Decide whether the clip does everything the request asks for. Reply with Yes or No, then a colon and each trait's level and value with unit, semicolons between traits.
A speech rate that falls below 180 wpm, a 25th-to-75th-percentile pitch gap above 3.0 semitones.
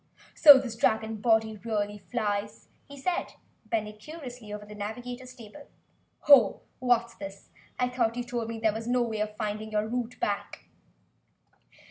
No: average, 155 wpm; average, 2.7 semitones